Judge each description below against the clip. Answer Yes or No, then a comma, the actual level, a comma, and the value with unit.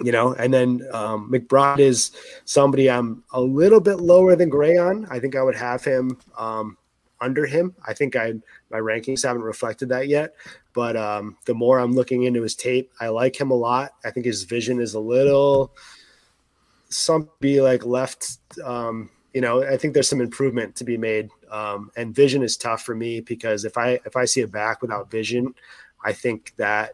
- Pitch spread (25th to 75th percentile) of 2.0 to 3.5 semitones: Yes, average, 2.9 semitones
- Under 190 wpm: No, average, 200 wpm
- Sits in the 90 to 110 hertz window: No, low, 125 Hz